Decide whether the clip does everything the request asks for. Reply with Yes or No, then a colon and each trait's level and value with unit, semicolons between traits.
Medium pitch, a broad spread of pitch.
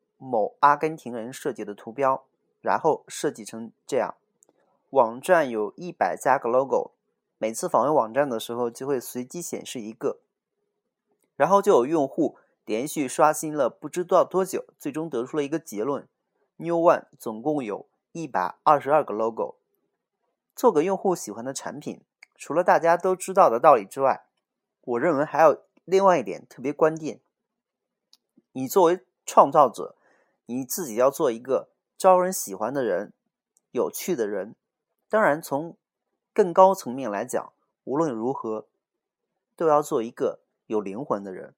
Yes: medium, 155 Hz; wide, 7.0 semitones